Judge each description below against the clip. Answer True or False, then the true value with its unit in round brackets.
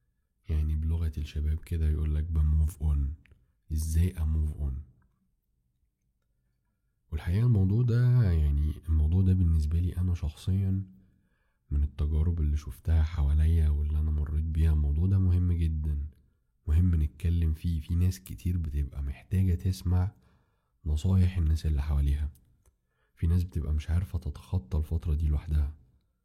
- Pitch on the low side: True (80 Hz)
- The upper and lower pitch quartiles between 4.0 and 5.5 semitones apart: False (3.1 semitones)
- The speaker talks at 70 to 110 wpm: False (130 wpm)